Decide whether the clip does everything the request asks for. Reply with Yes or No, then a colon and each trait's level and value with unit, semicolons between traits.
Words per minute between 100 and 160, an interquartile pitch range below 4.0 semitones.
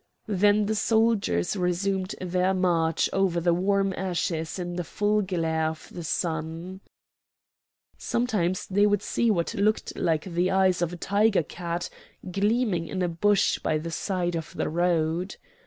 Yes: average, 155 wpm; average, 2.9 semitones